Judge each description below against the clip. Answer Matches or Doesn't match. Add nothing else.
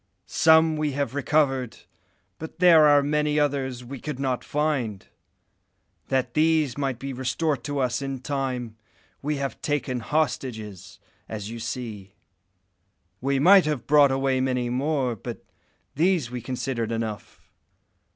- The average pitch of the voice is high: Doesn't match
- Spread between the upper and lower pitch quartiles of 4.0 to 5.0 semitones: Doesn't match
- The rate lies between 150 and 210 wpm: Doesn't match